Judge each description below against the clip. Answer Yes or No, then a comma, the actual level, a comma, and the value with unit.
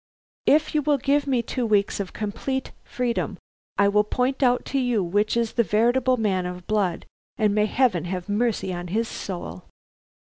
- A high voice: Yes, high, 215 Hz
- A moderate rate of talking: Yes, average, 180 wpm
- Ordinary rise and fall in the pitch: Yes, average, 4.2 semitones